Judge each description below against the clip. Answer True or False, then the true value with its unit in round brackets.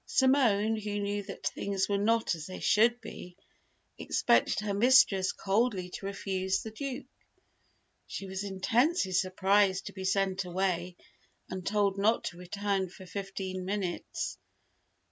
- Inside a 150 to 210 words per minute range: False (140 wpm)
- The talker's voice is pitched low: False (195 Hz)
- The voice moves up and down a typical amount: False (1.9 semitones)